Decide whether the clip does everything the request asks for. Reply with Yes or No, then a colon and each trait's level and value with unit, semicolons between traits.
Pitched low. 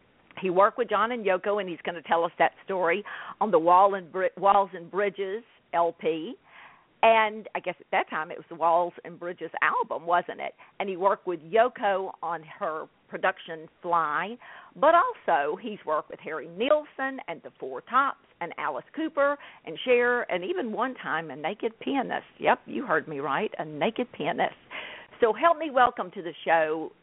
No: high, 195 Hz